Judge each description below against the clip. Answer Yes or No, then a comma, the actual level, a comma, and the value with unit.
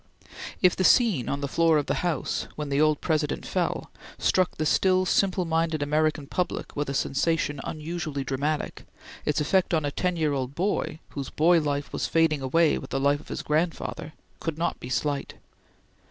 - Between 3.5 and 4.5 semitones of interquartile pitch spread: No, average, 2.7 semitones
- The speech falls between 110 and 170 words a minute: No, average, 185 wpm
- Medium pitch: Yes, medium, 155 Hz